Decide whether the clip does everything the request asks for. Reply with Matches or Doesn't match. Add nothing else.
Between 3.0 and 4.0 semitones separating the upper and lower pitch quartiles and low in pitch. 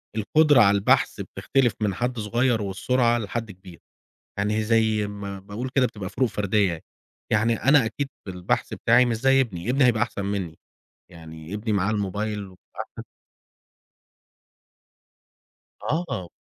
Matches